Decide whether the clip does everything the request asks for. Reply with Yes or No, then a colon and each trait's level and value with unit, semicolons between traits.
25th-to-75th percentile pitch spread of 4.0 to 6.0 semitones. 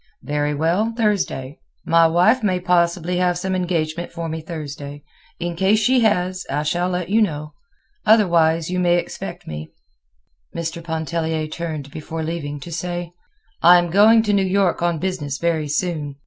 No: average, 2.7 semitones